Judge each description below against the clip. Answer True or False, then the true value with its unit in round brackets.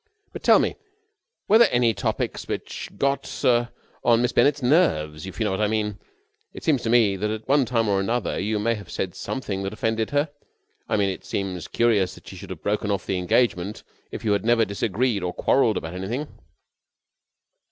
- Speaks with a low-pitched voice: True (110 Hz)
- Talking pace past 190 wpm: True (200 wpm)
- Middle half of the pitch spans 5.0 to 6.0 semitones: False (3.8 semitones)